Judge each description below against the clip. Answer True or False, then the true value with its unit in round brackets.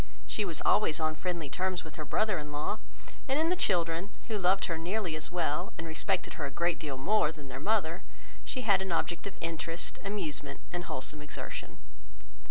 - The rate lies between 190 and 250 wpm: True (195 wpm)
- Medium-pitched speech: True (170 Hz)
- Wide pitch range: False (4.0 semitones)